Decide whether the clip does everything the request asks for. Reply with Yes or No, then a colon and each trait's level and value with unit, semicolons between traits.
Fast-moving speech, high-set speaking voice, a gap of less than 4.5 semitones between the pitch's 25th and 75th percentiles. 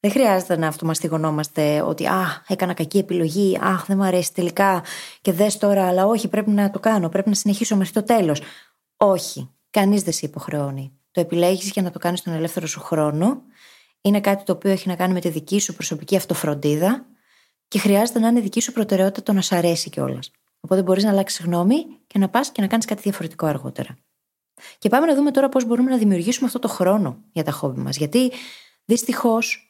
Yes: fast, 205 wpm; high, 195 Hz; average, 4.0 semitones